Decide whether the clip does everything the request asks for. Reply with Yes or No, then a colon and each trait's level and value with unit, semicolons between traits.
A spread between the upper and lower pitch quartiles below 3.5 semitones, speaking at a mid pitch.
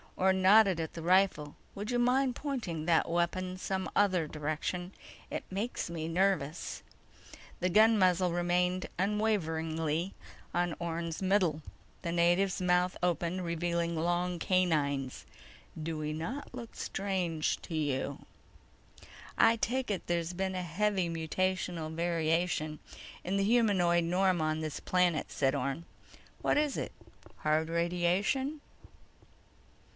Yes: average, 2.8 semitones; medium, 175 Hz